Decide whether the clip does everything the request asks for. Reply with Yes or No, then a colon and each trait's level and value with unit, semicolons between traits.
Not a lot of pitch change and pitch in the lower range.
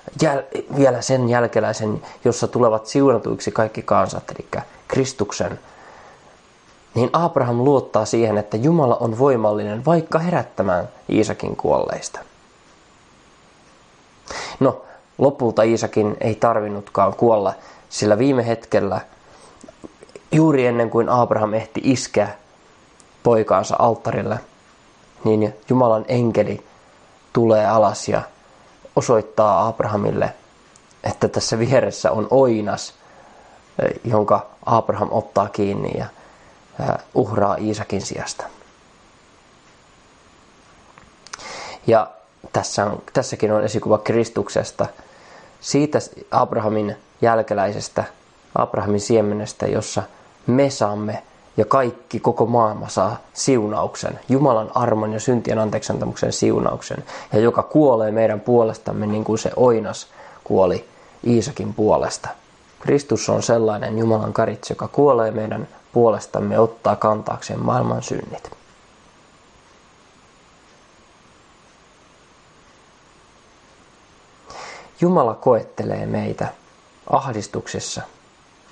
Yes: narrow, 2.2 semitones; low, 110 Hz